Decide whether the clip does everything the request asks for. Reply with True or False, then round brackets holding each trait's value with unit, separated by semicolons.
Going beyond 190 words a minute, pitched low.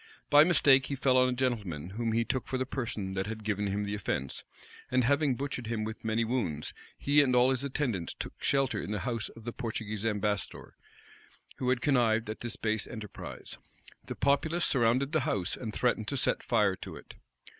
True (200 wpm; 115 Hz)